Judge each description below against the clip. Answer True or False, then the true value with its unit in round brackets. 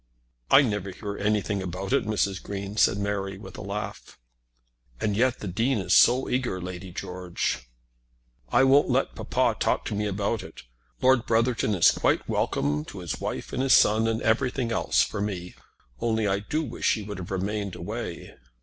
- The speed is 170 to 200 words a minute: True (180 wpm)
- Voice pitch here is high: False (105 Hz)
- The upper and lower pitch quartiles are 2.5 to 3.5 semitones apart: True (3.0 semitones)